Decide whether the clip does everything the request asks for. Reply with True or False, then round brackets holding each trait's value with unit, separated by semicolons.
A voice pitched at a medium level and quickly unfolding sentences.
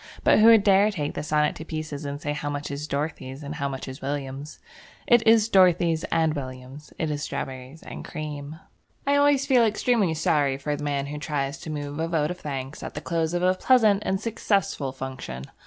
True (150 Hz; 215 wpm)